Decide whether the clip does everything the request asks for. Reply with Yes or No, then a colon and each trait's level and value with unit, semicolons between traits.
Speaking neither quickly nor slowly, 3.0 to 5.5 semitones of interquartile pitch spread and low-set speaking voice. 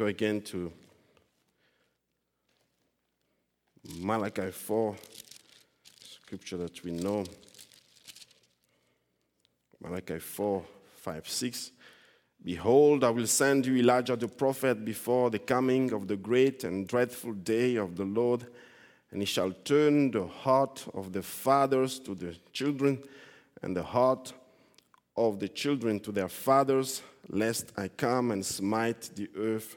No: slow, 120 wpm; average, 4.6 semitones; low, 110 Hz